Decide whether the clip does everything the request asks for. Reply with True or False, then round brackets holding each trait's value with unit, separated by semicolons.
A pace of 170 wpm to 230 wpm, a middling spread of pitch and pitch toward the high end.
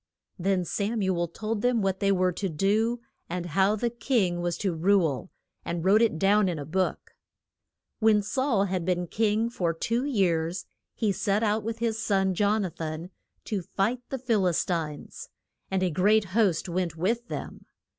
True (185 wpm; 3.8 semitones; 195 Hz)